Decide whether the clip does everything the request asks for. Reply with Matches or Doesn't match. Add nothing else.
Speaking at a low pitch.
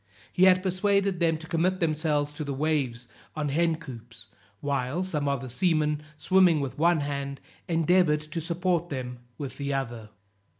Doesn't match